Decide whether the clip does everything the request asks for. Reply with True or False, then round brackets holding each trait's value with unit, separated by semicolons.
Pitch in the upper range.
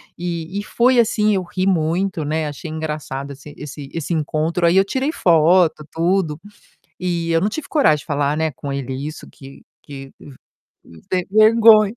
False (165 Hz)